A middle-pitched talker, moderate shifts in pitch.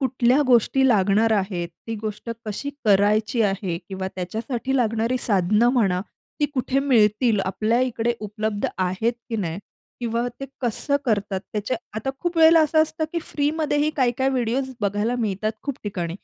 No: high, 225 Hz; average, 4.1 semitones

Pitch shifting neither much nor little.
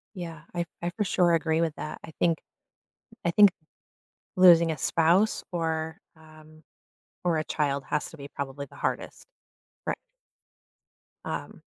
No: narrow, 1.7 semitones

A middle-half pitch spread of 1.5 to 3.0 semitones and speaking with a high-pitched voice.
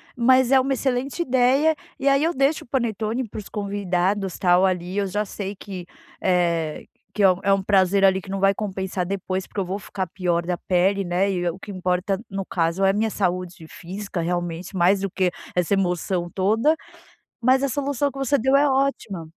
No: average, 4.6 semitones; high, 195 Hz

